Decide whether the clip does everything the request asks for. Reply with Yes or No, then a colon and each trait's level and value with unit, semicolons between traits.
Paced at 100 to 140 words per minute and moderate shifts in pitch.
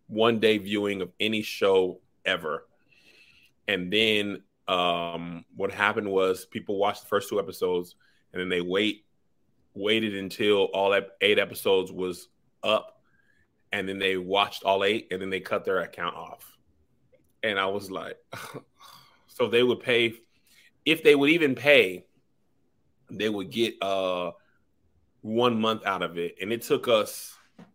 No: average, 150 wpm; average, 3.2 semitones